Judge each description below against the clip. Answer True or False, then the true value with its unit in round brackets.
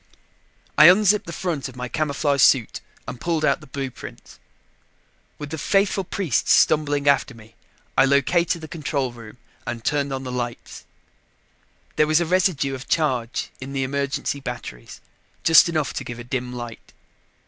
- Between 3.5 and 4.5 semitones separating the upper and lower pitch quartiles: True (4.0 semitones)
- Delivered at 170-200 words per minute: False (160 wpm)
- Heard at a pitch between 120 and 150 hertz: True (140 Hz)